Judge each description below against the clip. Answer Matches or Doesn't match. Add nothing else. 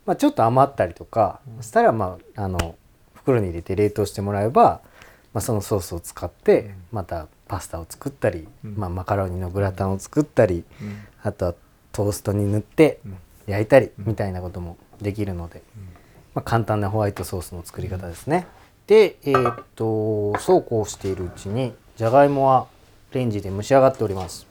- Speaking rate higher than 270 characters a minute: Matches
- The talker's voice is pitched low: Matches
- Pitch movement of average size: Matches